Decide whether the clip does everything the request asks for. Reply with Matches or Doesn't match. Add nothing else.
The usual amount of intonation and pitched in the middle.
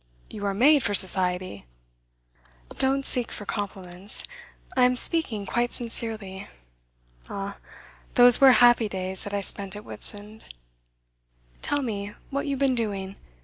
Doesn't match